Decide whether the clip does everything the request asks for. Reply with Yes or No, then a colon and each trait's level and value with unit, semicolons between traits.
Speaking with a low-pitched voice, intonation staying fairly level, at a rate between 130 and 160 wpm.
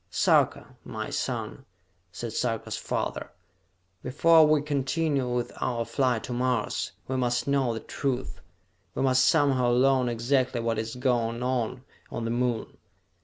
Yes: low, 125 Hz; narrow, 2.1 semitones; average, 140 wpm